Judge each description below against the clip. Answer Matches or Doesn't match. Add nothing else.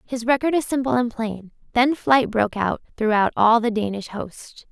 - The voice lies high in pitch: Matches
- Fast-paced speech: Doesn't match